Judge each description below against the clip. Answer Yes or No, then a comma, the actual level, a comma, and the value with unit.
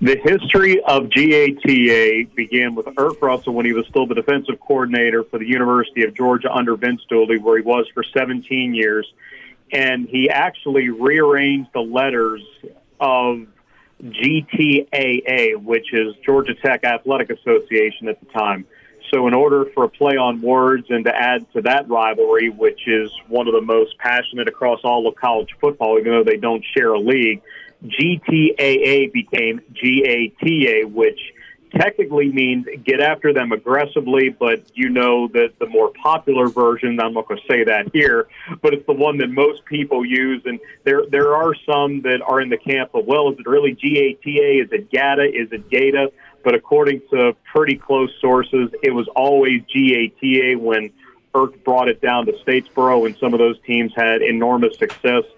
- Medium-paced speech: Yes, average, 180 wpm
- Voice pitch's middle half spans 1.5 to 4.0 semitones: Yes, average, 3.4 semitones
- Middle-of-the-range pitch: No, low, 130 Hz